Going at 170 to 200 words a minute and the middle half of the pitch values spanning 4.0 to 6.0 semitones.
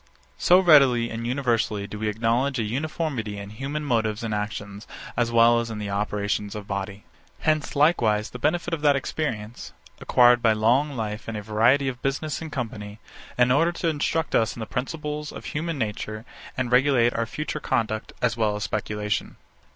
Yes: average, 180 wpm; average, 4.9 semitones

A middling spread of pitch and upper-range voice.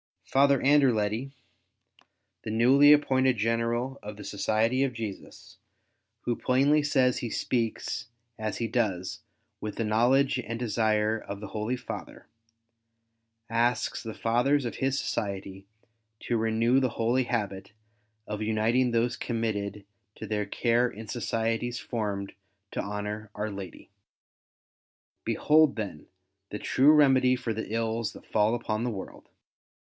No: average, 3.0 semitones; low, 115 Hz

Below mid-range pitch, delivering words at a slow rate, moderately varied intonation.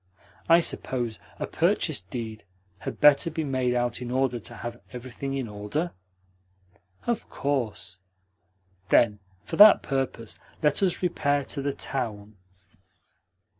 Yes: low, 130 Hz; slow, 130 wpm; average, 3.8 semitones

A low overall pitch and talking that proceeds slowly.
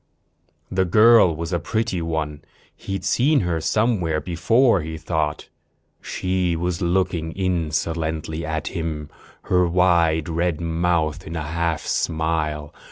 Yes: very low, 85 Hz; slow, 125 wpm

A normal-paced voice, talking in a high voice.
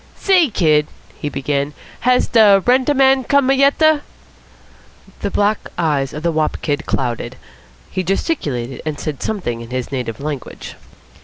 No: average, 155 wpm; medium, 155 Hz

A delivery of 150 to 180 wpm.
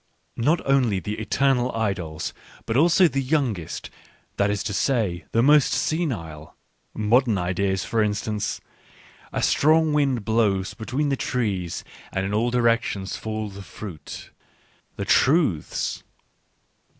No: slow, 135 wpm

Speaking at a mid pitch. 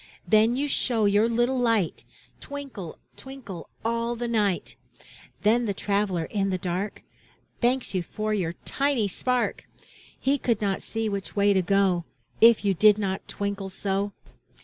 No: high, 210 Hz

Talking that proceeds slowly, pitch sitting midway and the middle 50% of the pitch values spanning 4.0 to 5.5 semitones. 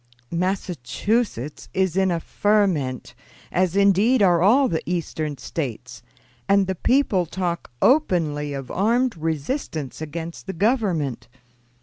Yes: slow, 115 wpm; medium, 180 Hz; average, 4.6 semitones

